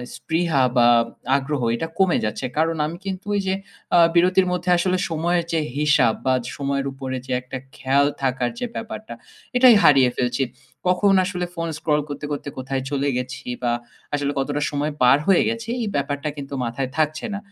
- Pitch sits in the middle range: Yes, medium, 145 Hz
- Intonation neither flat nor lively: Yes, average, 4.5 semitones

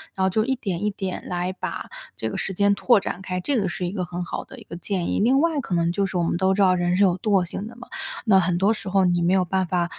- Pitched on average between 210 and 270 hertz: No, high, 190 Hz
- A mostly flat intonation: Yes, narrow, 2.3 semitones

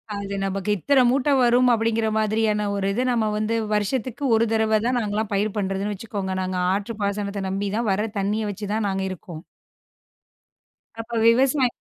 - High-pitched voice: Yes, high, 210 Hz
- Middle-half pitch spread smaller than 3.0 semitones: Yes, narrow, 2.4 semitones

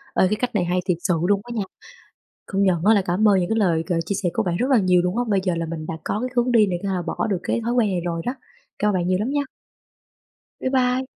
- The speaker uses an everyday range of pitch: Yes, average, 4.4 semitones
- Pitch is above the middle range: Yes, high, 195 Hz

